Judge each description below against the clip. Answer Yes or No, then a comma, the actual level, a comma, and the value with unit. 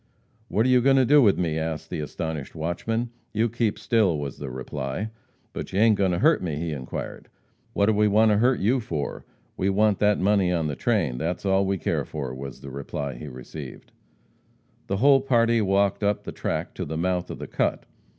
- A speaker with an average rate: No, fast, 215 wpm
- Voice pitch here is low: Yes, very low, 95 Hz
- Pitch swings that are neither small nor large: No, wide, 6.1 semitones